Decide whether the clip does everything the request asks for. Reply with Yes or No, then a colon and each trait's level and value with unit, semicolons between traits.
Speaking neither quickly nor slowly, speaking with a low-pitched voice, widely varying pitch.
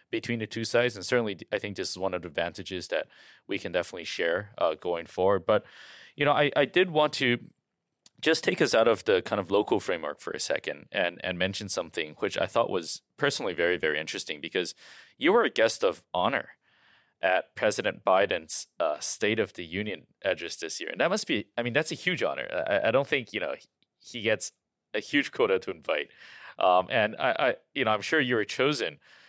No: fast, 220 wpm; low, 120 Hz; wide, 8.0 semitones